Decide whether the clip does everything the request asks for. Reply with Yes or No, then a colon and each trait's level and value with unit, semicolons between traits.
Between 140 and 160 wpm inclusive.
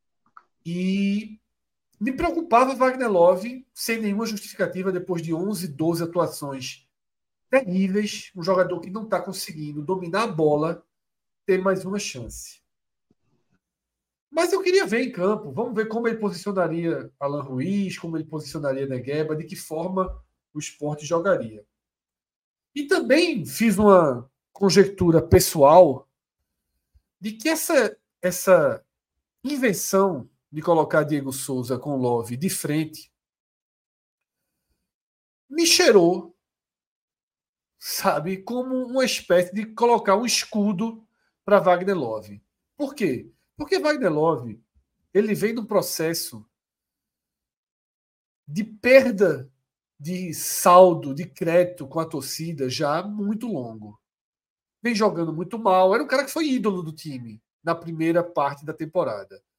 No: slow, 120 wpm